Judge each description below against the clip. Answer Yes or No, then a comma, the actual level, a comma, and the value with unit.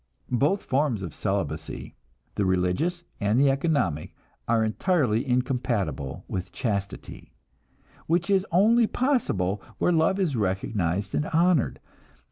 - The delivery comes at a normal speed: No, slow, 115 wpm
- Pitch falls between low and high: No, low, 125 Hz